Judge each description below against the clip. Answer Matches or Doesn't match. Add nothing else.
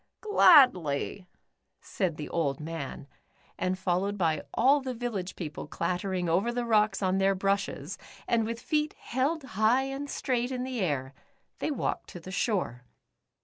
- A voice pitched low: Doesn't match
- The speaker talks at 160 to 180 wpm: Doesn't match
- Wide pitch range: Matches